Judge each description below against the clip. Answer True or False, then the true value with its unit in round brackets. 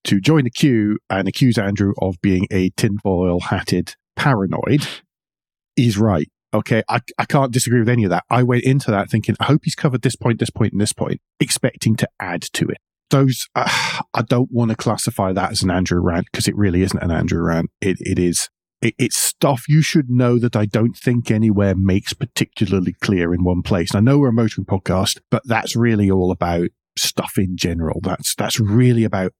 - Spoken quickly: True (210 wpm)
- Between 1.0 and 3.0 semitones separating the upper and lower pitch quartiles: False (4.4 semitones)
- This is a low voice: True (110 Hz)